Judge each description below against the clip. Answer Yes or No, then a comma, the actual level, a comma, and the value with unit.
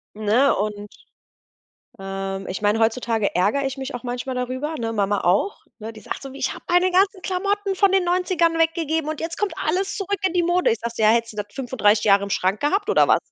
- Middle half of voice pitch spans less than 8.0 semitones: No, wide, 8.9 semitones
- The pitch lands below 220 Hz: No, very high, 260 Hz